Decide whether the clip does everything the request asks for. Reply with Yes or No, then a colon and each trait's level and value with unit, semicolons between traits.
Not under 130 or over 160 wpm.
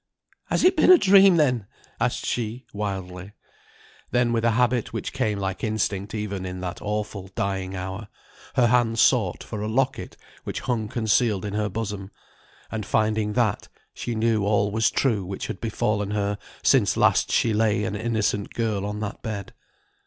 No: average, 170 wpm